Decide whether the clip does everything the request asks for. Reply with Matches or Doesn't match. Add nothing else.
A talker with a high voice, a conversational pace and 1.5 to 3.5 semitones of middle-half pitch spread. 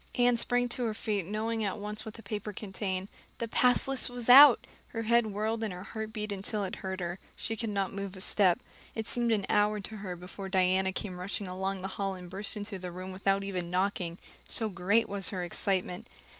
Doesn't match